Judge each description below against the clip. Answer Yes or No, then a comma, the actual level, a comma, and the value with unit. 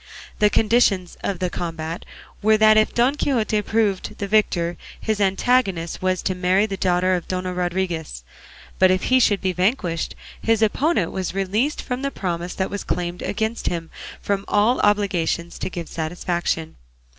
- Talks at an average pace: Yes, average, 170 wpm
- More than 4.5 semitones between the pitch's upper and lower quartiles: No, average, 3.5 semitones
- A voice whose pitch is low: No, high, 190 Hz